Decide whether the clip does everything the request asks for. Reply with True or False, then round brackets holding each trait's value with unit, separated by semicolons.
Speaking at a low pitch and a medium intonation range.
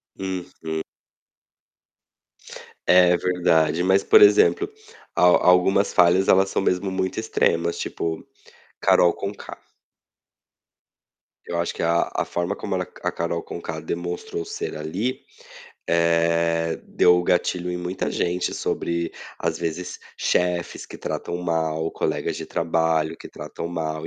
False (85 Hz; 1.6 semitones)